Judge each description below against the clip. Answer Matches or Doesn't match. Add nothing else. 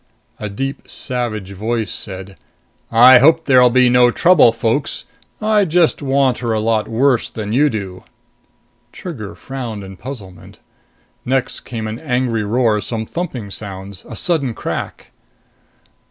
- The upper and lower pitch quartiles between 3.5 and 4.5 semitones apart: Matches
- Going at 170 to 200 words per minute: Doesn't match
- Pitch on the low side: Matches